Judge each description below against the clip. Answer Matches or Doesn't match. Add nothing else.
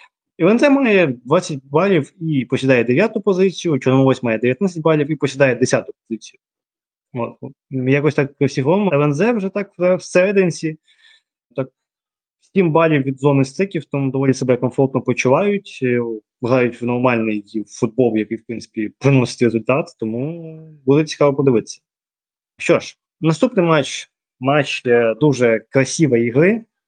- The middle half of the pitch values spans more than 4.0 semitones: Matches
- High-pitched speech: Doesn't match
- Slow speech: Doesn't match